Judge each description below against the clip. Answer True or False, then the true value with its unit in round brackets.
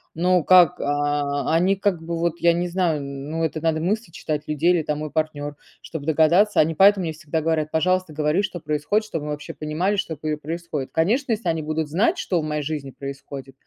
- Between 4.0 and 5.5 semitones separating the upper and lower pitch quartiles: False (2.8 semitones)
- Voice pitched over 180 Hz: False (160 Hz)